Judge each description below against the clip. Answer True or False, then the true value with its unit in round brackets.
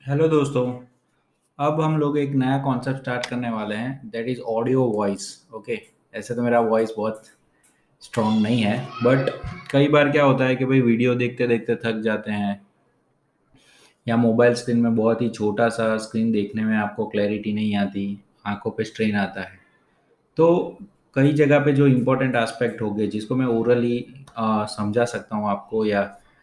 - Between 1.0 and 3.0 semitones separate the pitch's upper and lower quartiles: False (3.4 semitones)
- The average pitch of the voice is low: True (115 Hz)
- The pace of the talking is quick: False (175 wpm)